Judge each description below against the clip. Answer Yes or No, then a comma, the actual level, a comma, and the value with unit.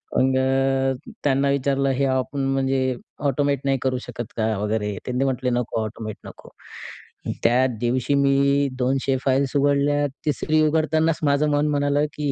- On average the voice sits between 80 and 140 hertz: Yes, low, 135 Hz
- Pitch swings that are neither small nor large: No, narrow, 1.7 semitones